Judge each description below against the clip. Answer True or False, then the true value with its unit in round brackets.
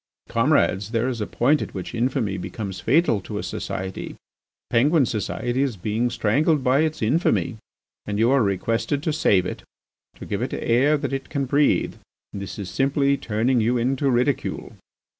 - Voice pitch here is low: True (120 Hz)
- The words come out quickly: False (170 wpm)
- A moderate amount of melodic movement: True (4.5 semitones)